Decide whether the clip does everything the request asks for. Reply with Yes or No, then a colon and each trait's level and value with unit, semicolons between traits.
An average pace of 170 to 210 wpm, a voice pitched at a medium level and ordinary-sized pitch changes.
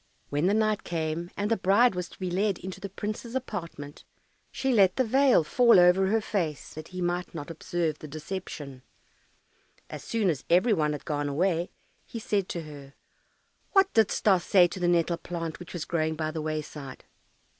Yes: average, 190 wpm; medium, 175 Hz; average, 4.6 semitones